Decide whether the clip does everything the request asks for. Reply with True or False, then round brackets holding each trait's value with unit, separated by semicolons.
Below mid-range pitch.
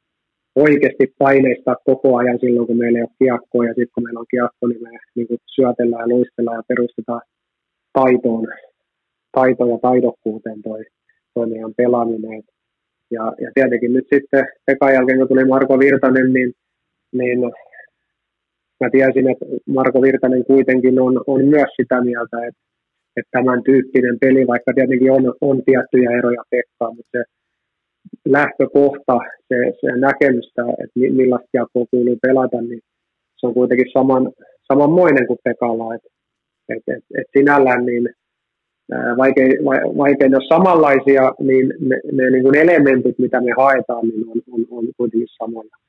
True (125 Hz)